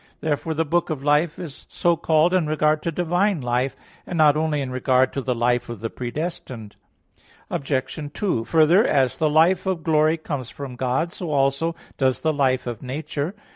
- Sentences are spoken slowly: No, average, 185 wpm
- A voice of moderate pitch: Yes, medium, 150 Hz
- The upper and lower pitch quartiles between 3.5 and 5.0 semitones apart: Yes, average, 3.9 semitones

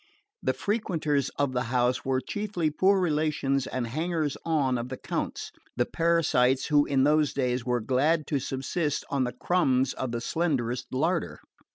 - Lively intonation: No, average, 4.0 semitones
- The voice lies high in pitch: No, medium, 140 Hz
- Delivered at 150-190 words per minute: Yes, average, 165 wpm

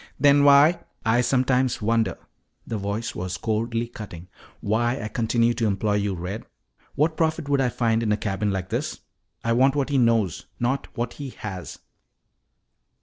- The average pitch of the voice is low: Yes, low, 115 Hz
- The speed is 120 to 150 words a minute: No, average, 170 wpm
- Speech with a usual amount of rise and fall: Yes, average, 4.0 semitones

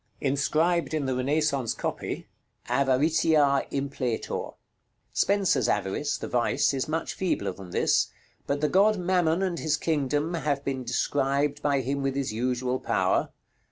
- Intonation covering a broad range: No, average, 3.3 semitones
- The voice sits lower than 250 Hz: Yes, medium, 140 Hz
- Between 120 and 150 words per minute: Yes, average, 140 wpm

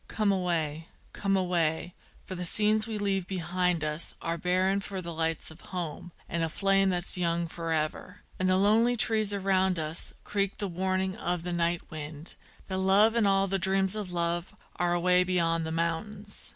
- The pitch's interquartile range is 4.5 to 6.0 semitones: No, narrow, 2.6 semitones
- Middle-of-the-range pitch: Yes, medium, 180 Hz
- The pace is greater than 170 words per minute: Yes, average, 185 wpm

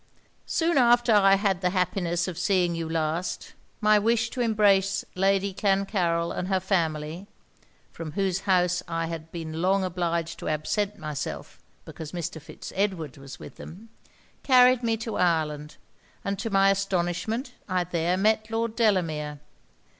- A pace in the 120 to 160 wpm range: Yes, average, 150 wpm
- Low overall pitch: No, medium, 185 Hz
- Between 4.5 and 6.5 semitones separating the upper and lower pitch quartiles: No, average, 3.7 semitones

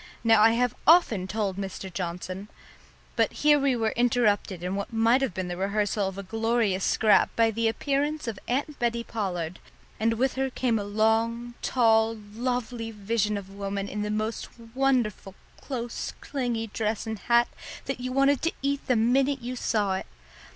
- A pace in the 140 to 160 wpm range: No, average, 180 wpm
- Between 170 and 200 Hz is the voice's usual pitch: No, high, 225 Hz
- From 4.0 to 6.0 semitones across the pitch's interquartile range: No, average, 3.4 semitones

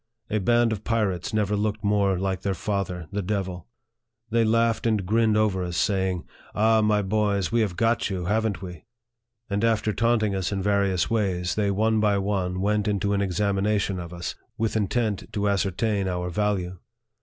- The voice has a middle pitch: No, low, 100 Hz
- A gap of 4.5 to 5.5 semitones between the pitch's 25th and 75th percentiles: No, narrow, 2.4 semitones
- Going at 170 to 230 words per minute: Yes, average, 180 wpm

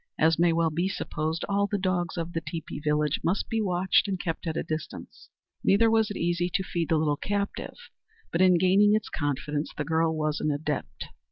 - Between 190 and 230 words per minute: Yes, fast, 205 wpm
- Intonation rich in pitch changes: No, average, 3.4 semitones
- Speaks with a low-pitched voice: No, medium, 170 Hz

